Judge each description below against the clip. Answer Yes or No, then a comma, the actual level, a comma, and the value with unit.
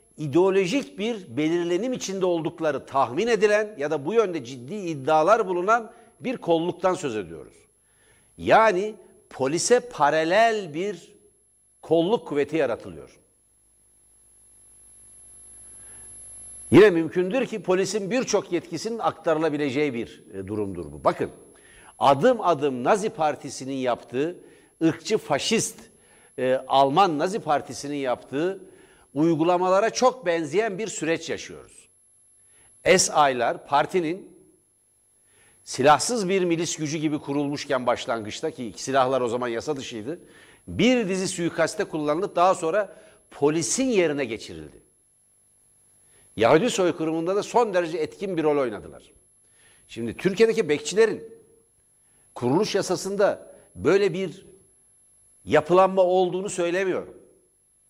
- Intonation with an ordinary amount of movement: No, wide, 6.5 semitones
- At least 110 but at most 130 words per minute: No, average, 100 wpm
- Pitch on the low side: No, medium, 165 Hz